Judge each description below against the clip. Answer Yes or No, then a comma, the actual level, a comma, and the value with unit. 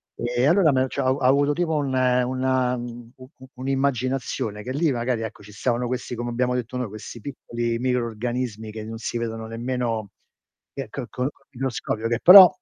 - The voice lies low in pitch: Yes, low, 125 Hz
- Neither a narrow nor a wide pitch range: No, narrow, 2.0 semitones